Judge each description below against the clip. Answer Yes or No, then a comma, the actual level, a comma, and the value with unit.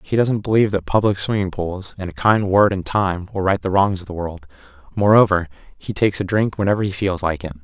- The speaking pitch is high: No, very low, 95 Hz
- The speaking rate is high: Yes, fast, 235 wpm